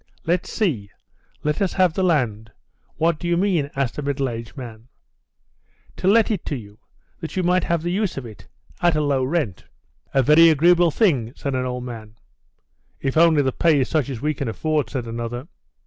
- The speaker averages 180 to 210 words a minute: Yes, average, 200 wpm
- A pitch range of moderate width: No, wide, 5.7 semitones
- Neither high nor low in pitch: Yes, medium, 145 Hz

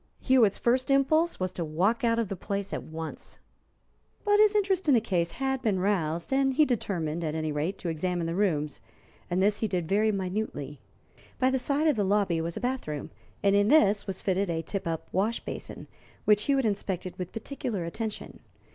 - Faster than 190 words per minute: Yes, average, 200 wpm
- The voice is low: No, high, 200 Hz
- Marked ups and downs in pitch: Yes, wide, 6.4 semitones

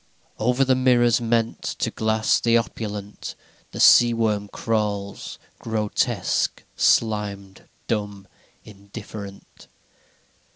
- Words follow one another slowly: Yes, slow, 95 wpm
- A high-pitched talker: No, low, 110 Hz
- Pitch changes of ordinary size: No, narrow, 2.2 semitones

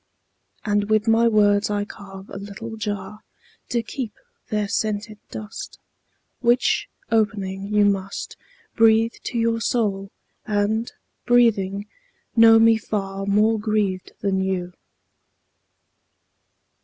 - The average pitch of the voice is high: Yes, high, 210 Hz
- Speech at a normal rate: No, slow, 110 wpm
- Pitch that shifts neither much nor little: No, narrow, 2.1 semitones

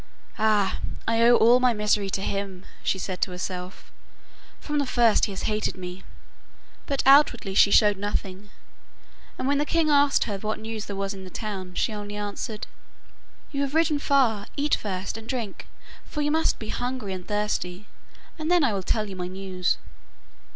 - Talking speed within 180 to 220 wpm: Yes, average, 185 wpm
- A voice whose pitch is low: No, high, 210 Hz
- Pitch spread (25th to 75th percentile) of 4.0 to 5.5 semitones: Yes, average, 4.7 semitones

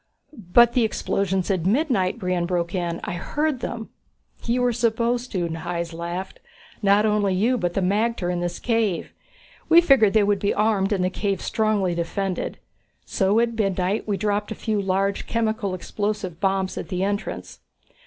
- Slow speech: No, average, 170 wpm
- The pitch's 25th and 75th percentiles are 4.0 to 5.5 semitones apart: No, average, 3.3 semitones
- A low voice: No, high, 200 Hz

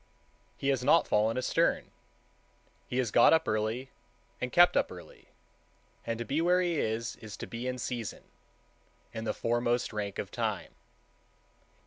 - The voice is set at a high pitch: No, low, 120 Hz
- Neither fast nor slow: Yes, average, 155 wpm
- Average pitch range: Yes, average, 3.2 semitones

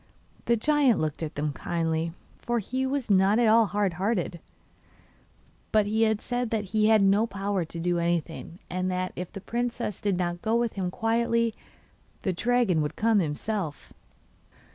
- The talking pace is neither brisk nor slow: Yes, average, 165 wpm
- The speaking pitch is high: Yes, high, 200 Hz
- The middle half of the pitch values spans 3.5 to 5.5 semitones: Yes, average, 4.8 semitones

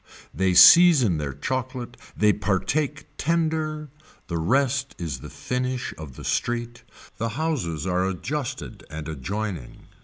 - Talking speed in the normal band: No, slow, 125 wpm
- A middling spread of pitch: No, wide, 8.0 semitones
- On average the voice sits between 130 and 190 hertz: No, low, 120 Hz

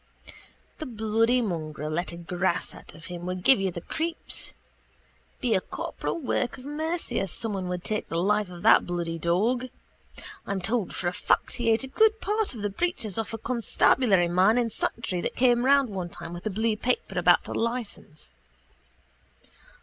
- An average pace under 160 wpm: No, average, 185 wpm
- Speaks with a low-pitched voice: No, high, 210 Hz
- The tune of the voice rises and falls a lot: Yes, wide, 5.7 semitones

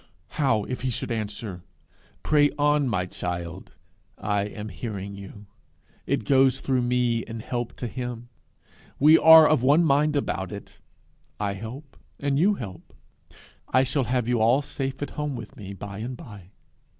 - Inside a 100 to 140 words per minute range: No, average, 160 wpm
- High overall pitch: No, low, 120 Hz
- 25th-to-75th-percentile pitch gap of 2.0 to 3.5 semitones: No, average, 5.0 semitones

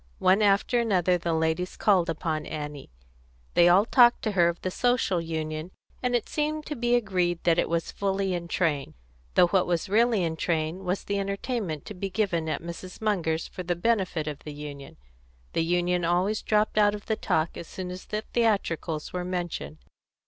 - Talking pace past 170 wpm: Yes, average, 190 wpm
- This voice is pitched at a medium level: Yes, medium, 180 Hz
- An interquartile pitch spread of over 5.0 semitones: No, average, 3.8 semitones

